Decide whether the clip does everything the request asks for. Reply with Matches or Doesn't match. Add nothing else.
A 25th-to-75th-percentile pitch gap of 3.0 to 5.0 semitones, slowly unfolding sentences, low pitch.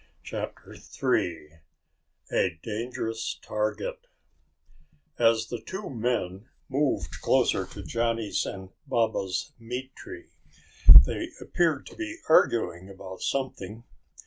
Doesn't match